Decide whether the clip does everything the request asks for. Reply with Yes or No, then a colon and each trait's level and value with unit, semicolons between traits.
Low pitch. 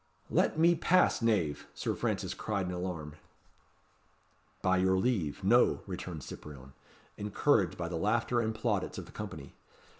Yes: very low, 95 Hz